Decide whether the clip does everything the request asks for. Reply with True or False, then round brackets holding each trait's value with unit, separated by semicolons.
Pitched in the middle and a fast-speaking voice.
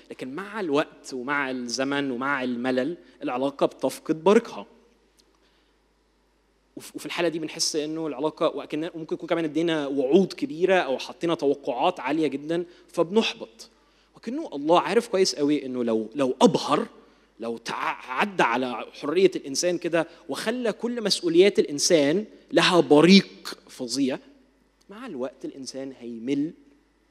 False (160 Hz; 120 wpm)